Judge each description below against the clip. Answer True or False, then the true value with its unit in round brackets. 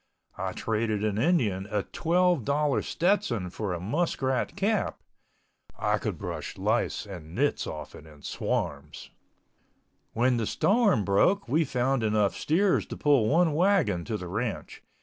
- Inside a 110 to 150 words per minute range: True (140 wpm)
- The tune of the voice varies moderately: False (8.4 semitones)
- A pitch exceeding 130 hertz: False (120 Hz)